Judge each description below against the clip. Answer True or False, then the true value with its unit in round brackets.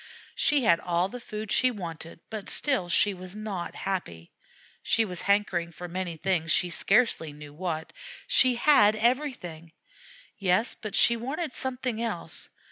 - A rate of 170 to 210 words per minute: False (150 wpm)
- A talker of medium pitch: False (195 Hz)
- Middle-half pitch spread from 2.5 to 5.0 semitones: False (5.6 semitones)